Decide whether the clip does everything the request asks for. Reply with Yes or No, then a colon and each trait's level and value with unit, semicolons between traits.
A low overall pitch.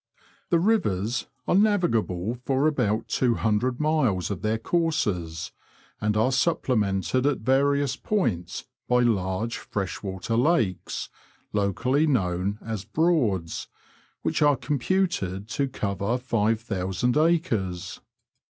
Yes: low, 115 Hz